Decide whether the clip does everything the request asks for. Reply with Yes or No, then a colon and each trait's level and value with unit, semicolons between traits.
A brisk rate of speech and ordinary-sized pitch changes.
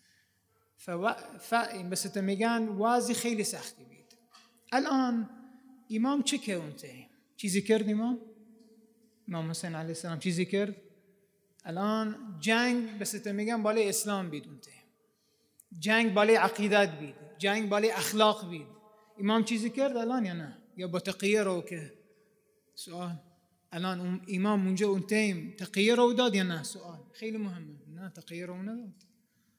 Yes: fast, 140 wpm; average, 3.7 semitones